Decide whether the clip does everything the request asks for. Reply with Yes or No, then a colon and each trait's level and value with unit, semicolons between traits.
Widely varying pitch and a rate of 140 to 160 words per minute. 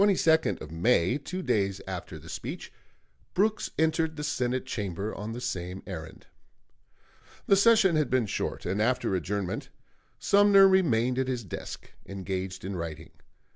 Yes: wide, 9.0 semitones; average, 155 wpm